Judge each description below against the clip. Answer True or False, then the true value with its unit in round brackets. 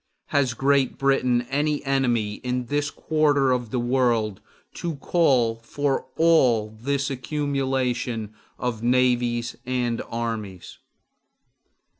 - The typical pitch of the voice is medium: False (125 Hz)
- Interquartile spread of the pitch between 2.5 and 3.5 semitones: True (2.9 semitones)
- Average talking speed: False (105 wpm)